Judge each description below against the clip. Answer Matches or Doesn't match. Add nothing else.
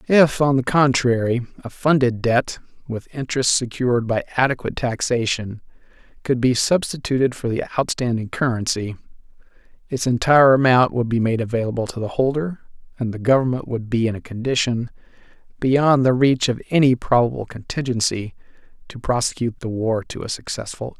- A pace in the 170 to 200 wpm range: Doesn't match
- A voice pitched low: Matches